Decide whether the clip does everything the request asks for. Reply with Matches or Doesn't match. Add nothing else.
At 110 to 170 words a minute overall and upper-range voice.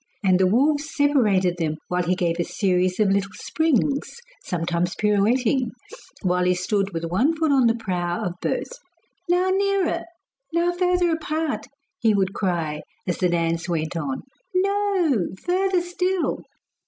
Matches